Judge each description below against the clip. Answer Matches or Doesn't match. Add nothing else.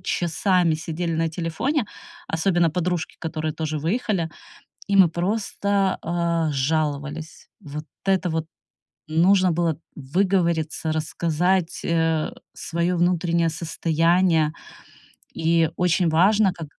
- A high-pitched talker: Doesn't match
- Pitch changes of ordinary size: Doesn't match